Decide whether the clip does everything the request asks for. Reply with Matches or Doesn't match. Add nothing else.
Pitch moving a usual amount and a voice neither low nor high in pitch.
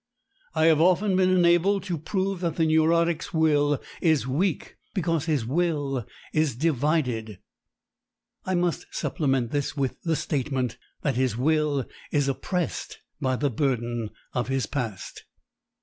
Matches